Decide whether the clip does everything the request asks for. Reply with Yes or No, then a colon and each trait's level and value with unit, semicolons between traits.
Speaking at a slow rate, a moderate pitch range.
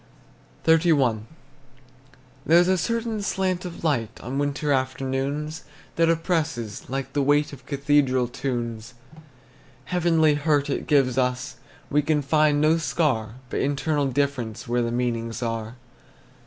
Yes: slow, 130 wpm; average, 3.9 semitones